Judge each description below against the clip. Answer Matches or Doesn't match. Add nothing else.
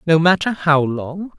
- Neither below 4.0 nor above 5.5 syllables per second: Matches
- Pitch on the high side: Doesn't match